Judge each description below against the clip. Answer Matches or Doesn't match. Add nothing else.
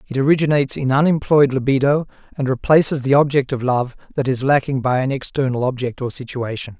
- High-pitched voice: Doesn't match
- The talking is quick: Doesn't match